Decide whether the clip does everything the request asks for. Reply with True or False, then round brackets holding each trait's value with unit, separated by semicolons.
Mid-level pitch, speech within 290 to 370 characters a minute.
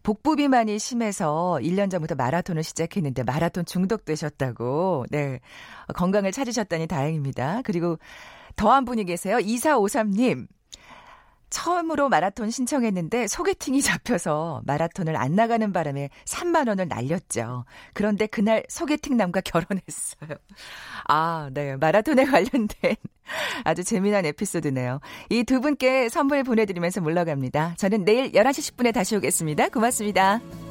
False (200 Hz; 315 characters per minute)